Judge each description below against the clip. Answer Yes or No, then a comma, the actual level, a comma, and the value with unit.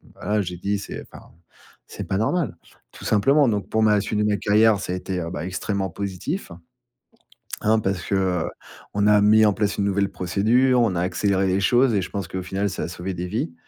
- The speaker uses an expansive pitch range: No, narrow, 2.4 semitones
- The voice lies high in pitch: No, low, 100 Hz